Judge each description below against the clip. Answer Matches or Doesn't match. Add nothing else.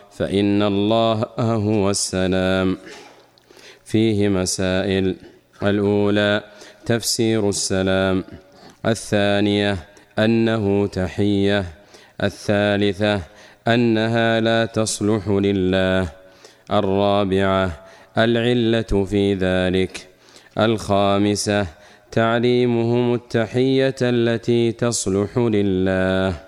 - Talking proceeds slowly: Matches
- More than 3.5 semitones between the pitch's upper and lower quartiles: Doesn't match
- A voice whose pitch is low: Matches